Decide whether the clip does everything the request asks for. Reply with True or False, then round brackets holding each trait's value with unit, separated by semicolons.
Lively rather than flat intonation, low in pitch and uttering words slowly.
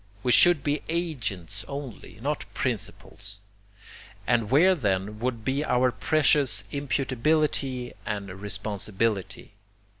True (5.7 semitones; 125 Hz; 100 wpm)